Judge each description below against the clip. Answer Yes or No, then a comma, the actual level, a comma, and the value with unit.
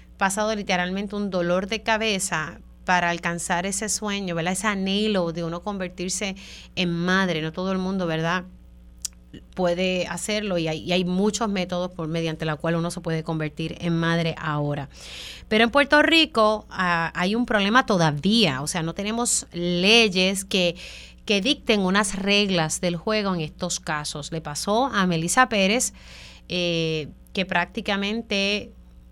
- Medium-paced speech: Yes, average, 155 wpm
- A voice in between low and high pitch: Yes, medium, 180 Hz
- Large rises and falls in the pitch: No, average, 3.7 semitones